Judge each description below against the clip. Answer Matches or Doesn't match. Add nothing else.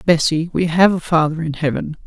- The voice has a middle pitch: Matches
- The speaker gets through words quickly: Doesn't match